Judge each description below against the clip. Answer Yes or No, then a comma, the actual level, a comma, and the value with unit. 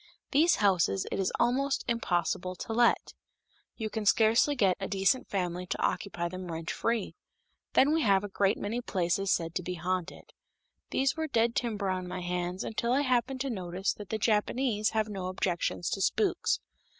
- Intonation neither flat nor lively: Yes, average, 4.5 semitones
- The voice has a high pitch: Yes, high, 200 Hz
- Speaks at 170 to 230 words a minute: Yes, average, 180 wpm